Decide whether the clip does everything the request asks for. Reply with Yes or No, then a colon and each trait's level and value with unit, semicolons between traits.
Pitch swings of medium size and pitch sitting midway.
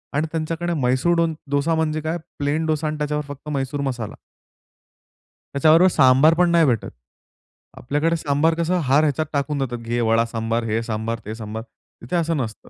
Yes: average, 4.9 semitones; medium, 145 Hz